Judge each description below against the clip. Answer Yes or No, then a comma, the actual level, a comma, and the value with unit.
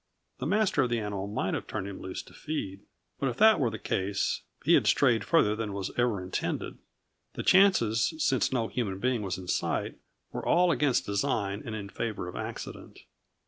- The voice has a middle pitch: No, low, 110 Hz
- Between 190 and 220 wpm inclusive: Yes, average, 195 wpm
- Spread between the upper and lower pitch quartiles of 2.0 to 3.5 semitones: No, average, 5.1 semitones